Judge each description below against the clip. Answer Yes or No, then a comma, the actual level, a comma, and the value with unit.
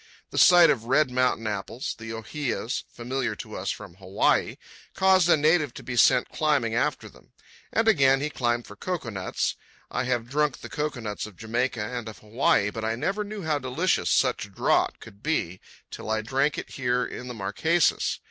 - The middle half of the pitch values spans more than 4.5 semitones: Yes, average, 5.2 semitones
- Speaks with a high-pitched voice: No, low, 125 Hz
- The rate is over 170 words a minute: Yes, average, 185 wpm